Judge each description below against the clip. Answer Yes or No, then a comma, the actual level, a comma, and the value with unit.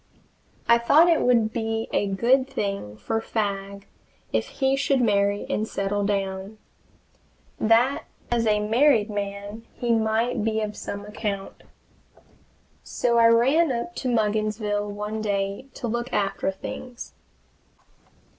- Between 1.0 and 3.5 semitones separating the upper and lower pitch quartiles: Yes, average, 2.7 semitones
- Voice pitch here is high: Yes, high, 220 Hz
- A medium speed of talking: No, slow, 130 wpm